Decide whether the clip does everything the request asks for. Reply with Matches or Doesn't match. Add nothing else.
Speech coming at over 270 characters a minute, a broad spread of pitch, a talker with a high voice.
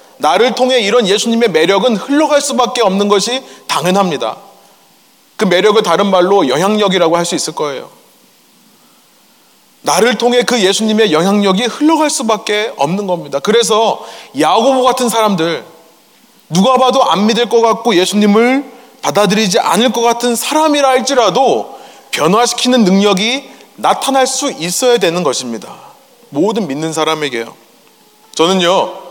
Doesn't match